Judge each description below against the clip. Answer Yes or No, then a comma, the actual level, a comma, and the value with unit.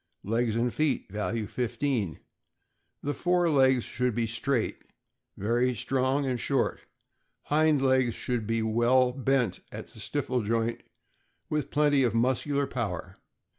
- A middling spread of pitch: Yes, average, 3.1 semitones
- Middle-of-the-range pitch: No, low, 125 Hz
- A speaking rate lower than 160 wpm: Yes, slow, 135 wpm